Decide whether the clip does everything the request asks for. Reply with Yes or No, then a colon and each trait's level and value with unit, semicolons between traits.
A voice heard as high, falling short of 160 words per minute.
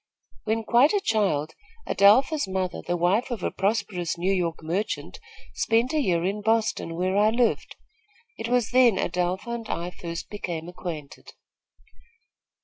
Yes: high, 195 Hz; average, 145 wpm